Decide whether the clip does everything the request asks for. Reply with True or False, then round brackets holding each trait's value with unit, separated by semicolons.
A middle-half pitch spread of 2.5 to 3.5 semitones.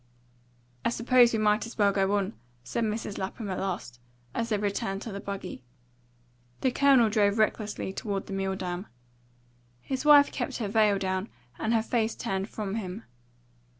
True (2.8 semitones)